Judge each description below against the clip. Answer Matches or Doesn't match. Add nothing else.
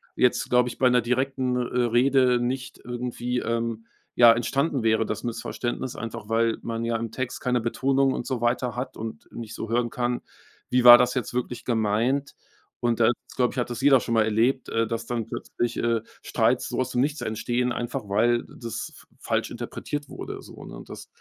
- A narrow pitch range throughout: Matches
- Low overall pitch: Matches